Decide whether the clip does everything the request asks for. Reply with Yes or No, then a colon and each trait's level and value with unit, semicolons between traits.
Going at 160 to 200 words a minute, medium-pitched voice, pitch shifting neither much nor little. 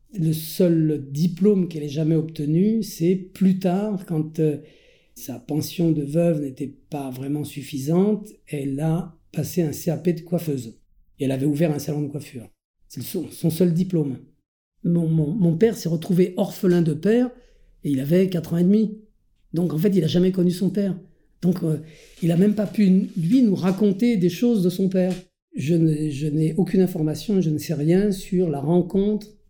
Yes: average, 190 wpm; medium, 170 Hz; average, 3.7 semitones